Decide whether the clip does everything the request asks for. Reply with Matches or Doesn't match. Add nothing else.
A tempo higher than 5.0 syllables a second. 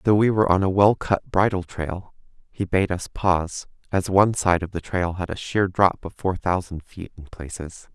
Doesn't match